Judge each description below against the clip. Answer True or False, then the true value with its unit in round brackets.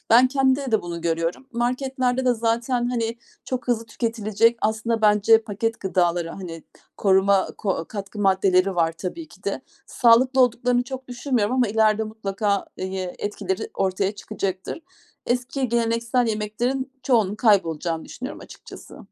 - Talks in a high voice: True (220 Hz)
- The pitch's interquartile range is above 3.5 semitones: True (4.1 semitones)